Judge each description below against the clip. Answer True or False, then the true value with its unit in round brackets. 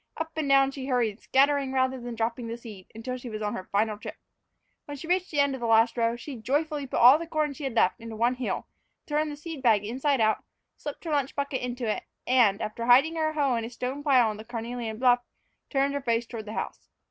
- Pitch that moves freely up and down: False (3.6 semitones)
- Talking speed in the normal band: False (245 wpm)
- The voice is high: True (250 Hz)